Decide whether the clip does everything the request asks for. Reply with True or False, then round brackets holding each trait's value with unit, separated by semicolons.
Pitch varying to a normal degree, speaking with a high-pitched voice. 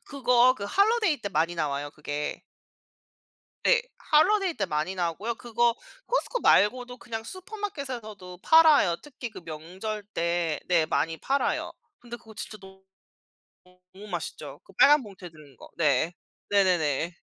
False (7.2 semitones; 205 Hz)